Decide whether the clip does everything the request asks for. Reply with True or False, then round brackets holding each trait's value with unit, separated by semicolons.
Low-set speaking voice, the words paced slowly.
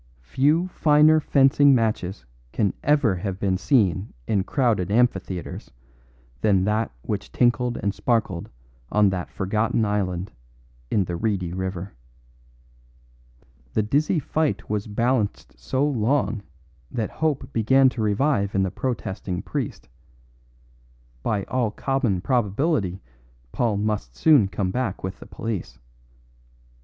True (105 Hz; 120 wpm)